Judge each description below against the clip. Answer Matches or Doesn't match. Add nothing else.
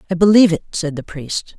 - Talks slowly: Doesn't match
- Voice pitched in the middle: Matches